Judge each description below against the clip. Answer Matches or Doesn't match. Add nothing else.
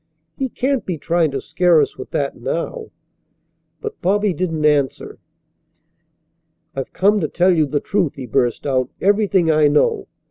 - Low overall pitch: Doesn't match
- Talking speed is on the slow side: Doesn't match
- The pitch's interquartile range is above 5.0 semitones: Matches